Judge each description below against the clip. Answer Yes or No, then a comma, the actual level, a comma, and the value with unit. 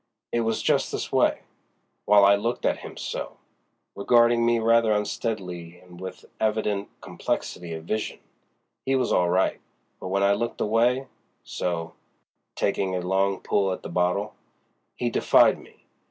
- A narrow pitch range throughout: No, average, 4.0 semitones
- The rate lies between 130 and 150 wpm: Yes, average, 140 wpm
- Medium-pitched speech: No, low, 100 Hz